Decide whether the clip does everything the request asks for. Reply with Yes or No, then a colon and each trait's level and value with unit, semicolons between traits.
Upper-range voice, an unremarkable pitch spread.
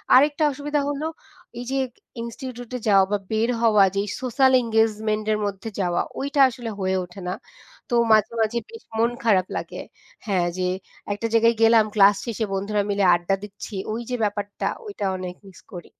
Yes: high, 220 Hz; average, 3.3 semitones